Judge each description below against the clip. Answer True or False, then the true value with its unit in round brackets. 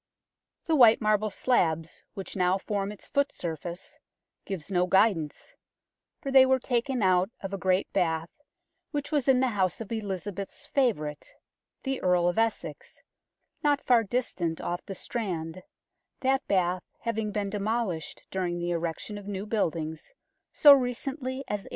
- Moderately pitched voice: False (200 Hz)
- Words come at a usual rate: True (150 wpm)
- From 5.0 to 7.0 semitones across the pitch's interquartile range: True (5.6 semitones)